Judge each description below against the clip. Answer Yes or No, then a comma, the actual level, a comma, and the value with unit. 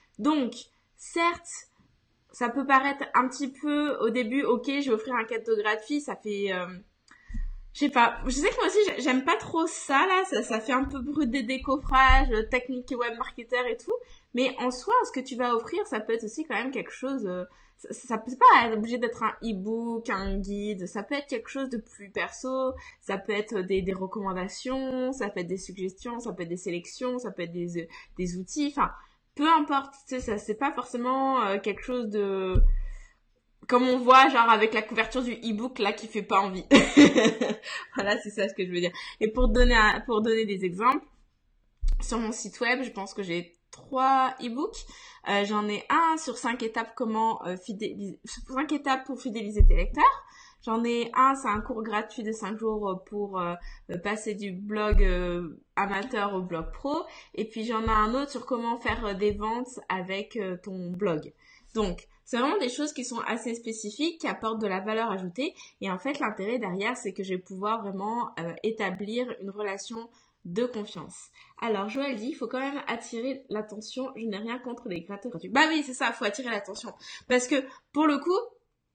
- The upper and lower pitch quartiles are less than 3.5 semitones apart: No, average, 4.3 semitones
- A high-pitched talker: Yes, high, 230 Hz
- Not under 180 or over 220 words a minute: Yes, average, 205 wpm